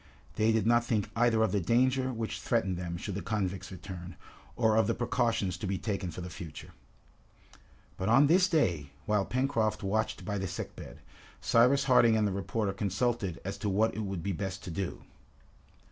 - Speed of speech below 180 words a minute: No, average, 190 wpm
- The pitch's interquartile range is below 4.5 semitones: Yes, average, 3.7 semitones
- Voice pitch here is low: Yes, low, 105 Hz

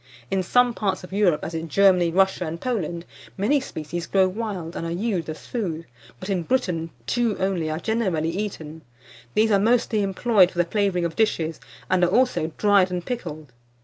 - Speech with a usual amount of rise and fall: Yes, average, 4.1 semitones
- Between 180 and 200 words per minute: Yes, average, 185 wpm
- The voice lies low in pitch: No, medium, 185 Hz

